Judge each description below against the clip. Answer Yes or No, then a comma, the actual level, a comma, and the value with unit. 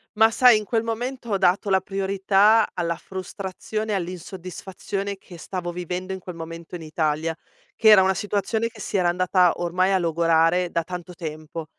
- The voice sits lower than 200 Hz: Yes, medium, 185 Hz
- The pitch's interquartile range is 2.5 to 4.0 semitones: Yes, average, 2.9 semitones